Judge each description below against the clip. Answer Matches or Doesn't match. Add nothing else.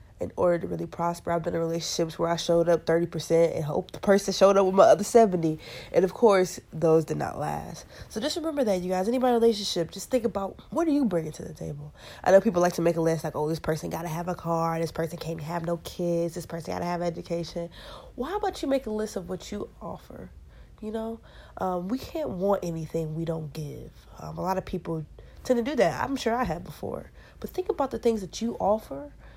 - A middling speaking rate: Doesn't match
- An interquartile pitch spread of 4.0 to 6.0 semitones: Matches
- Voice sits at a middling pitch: Matches